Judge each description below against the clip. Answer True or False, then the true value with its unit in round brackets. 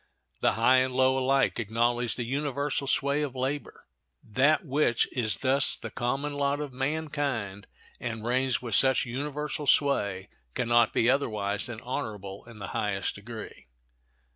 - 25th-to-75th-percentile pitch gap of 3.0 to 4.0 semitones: True (3.7 semitones)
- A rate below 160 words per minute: True (150 wpm)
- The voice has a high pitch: False (130 Hz)